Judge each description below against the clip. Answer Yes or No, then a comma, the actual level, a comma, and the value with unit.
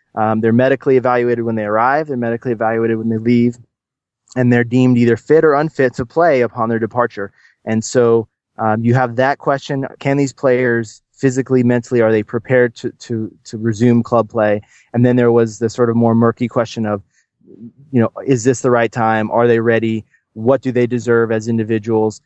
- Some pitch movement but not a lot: No, narrow, 2.1 semitones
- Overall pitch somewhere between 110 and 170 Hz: Yes, low, 120 Hz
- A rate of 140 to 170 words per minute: No, fast, 205 wpm